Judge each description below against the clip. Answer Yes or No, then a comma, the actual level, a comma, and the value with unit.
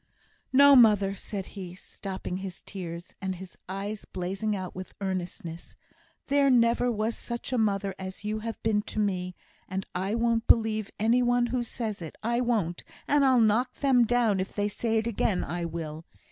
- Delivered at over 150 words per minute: Yes, average, 180 wpm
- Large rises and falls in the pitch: No, average, 3.9 semitones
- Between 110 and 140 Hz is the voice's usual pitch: No, high, 210 Hz